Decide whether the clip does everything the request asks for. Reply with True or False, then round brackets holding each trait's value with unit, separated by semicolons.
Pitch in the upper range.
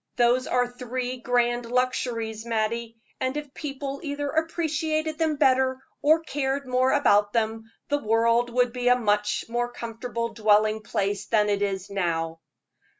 True (245 Hz)